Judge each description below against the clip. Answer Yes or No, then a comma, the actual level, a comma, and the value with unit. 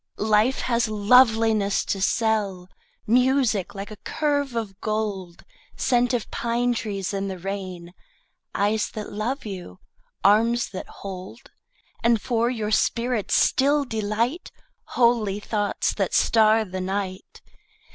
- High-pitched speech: Yes, high, 215 Hz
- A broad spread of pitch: No, average, 3.1 semitones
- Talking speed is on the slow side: Yes, slow, 125 wpm